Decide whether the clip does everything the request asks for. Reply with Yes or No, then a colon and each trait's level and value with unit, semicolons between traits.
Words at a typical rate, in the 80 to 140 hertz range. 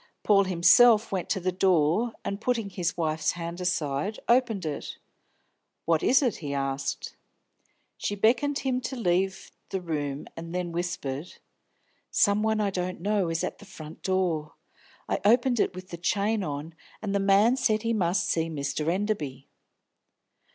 No: average, 160 wpm; medium, 185 Hz